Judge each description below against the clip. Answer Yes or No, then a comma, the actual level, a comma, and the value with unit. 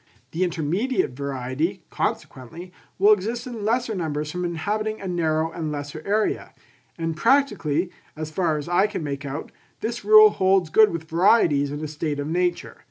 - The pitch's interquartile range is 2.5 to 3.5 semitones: No, average, 5.3 semitones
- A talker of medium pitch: Yes, medium, 170 Hz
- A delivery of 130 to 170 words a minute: Yes, average, 165 wpm